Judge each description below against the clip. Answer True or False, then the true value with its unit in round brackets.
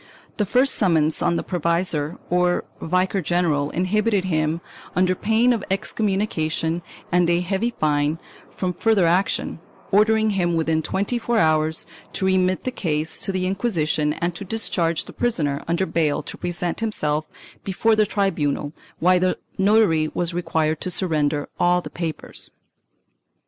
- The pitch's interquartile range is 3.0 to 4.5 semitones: True (3.7 semitones)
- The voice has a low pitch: False (180 Hz)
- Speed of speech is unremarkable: True (150 wpm)